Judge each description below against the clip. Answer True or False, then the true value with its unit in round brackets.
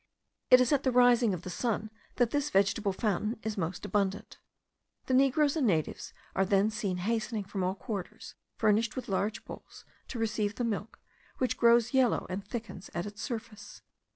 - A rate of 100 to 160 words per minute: False (180 wpm)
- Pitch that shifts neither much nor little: True (3.4 semitones)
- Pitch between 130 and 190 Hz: False (220 Hz)